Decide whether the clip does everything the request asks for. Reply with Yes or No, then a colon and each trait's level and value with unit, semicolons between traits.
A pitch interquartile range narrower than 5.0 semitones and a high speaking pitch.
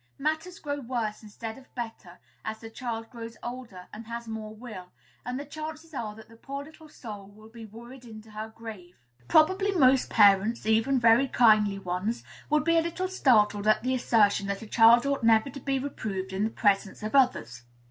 Yes: average, 4.0 semitones; high, 230 Hz